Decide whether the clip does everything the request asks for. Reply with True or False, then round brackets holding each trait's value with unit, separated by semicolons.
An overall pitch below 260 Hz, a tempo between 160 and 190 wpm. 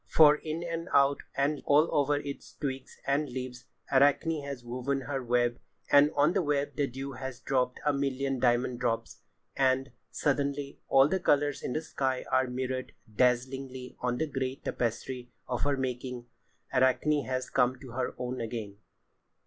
True (135 Hz; 165 wpm)